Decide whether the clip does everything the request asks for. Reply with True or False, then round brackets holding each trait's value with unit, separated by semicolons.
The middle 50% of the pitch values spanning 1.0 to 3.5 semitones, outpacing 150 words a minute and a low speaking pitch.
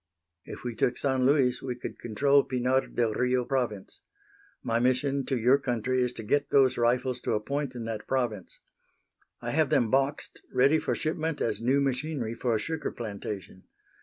True (2.7 semitones; 180 wpm; 125 Hz)